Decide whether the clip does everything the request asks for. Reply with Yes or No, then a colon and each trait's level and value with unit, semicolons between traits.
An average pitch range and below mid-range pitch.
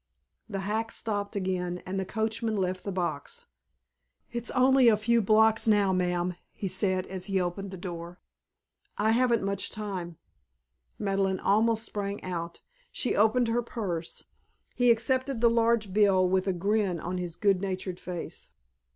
No: average, 3.4 semitones; high, 200 Hz